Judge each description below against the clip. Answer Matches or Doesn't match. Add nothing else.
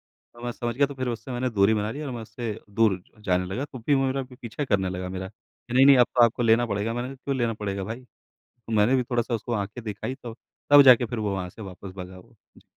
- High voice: Doesn't match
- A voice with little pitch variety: Doesn't match